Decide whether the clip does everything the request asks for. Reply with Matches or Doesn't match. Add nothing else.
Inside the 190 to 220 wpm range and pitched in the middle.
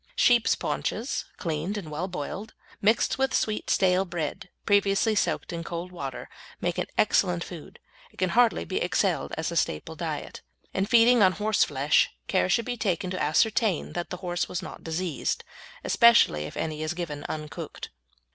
Doesn't match